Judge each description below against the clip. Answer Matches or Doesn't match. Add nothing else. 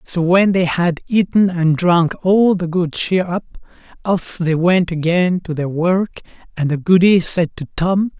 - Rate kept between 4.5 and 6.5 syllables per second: Doesn't match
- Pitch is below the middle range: Doesn't match